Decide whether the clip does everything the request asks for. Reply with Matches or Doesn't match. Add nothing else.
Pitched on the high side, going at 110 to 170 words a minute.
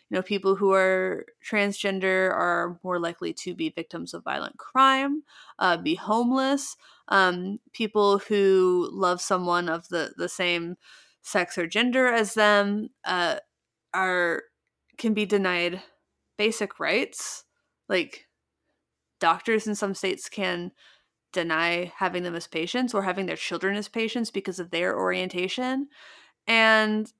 Matches